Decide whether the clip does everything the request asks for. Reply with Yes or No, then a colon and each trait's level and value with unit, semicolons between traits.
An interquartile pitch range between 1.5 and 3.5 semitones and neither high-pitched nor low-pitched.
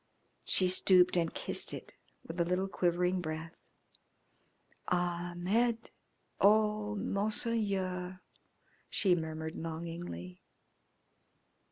Yes: average, 2.8 semitones; medium, 180 Hz